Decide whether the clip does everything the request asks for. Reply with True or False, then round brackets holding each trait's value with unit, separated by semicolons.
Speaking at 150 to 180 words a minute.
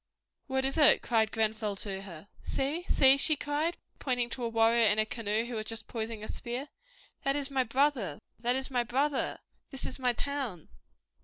False (190 wpm)